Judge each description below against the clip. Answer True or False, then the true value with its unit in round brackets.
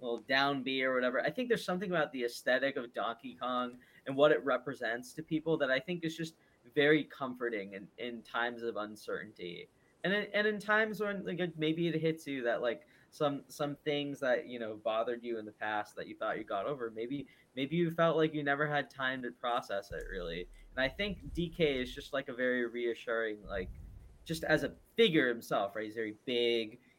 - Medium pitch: False (130 Hz)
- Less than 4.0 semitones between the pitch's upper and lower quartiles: False (4.9 semitones)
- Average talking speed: False (215 wpm)